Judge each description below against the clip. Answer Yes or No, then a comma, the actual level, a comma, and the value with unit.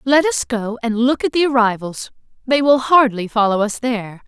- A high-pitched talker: Yes, high, 240 Hz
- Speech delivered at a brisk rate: No, average, 195 wpm